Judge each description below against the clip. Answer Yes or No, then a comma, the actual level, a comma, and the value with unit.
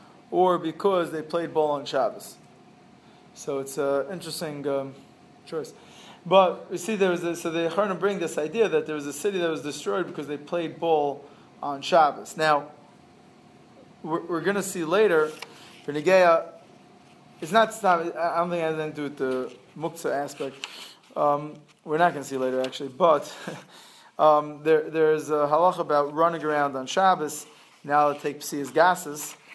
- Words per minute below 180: No, average, 185 wpm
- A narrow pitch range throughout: No, average, 3.4 semitones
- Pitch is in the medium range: Yes, medium, 155 Hz